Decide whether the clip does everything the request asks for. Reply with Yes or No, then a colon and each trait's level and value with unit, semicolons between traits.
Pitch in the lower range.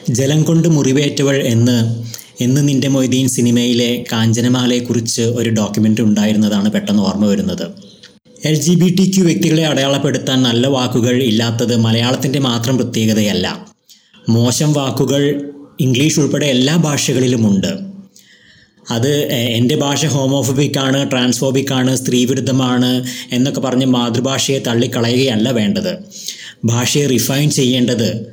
Yes: low, 130 Hz